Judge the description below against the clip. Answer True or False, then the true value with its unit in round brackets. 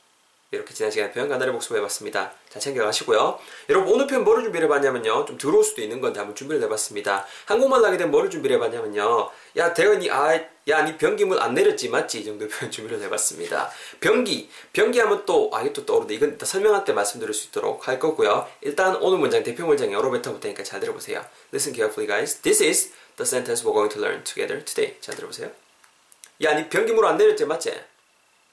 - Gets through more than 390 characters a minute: True (530 characters per minute)